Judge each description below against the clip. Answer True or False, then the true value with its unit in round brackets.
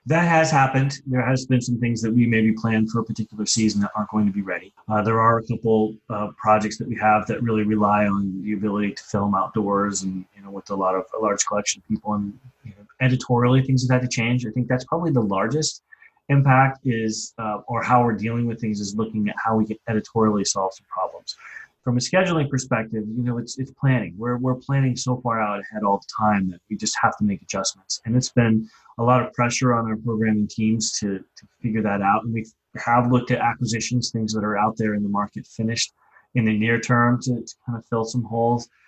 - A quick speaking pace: True (240 wpm)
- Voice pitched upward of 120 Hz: False (115 Hz)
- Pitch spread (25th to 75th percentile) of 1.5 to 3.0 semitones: True (2.6 semitones)